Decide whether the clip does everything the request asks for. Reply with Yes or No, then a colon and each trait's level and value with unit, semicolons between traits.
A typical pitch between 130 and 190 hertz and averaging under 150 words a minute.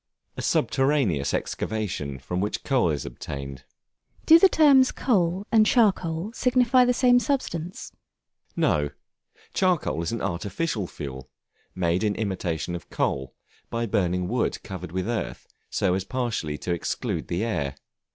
No: low, 105 Hz; average, 140 wpm